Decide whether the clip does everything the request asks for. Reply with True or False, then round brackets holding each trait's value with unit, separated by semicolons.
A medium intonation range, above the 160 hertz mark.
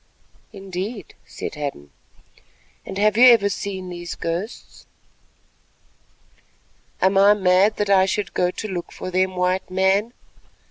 False (2.1 semitones; 190 Hz)